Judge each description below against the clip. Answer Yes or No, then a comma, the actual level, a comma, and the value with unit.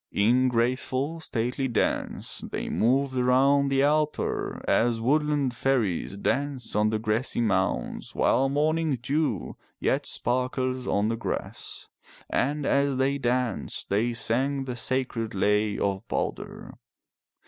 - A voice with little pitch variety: No, average, 3.3 semitones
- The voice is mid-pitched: No, low, 130 Hz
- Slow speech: Yes, slow, 125 wpm